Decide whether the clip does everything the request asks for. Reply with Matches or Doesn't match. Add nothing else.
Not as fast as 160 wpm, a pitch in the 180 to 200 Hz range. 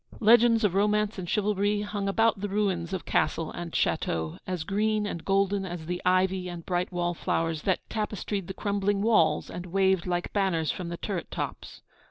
Doesn't match